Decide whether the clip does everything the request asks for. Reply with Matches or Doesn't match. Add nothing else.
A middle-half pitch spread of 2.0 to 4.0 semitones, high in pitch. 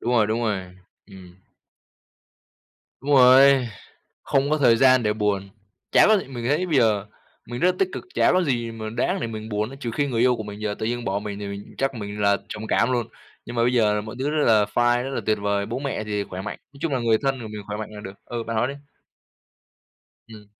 Doesn't match